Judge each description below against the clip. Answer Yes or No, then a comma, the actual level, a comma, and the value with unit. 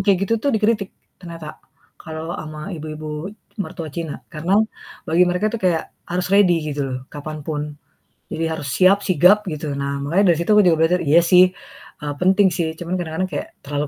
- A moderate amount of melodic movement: Yes, average, 3.3 semitones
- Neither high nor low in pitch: Yes, medium, 170 Hz